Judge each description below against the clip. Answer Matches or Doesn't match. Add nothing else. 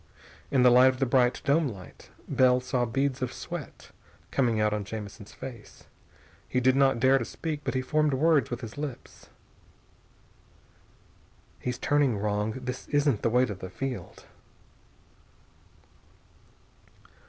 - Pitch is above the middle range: Doesn't match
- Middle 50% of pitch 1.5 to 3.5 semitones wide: Matches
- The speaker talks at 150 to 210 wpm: Doesn't match